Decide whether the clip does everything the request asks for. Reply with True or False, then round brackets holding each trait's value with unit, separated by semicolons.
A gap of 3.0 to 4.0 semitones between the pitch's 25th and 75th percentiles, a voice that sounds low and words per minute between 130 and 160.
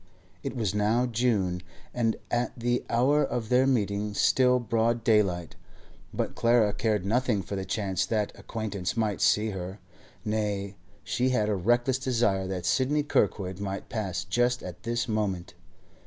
True (3.6 semitones; 110 Hz; 155 wpm)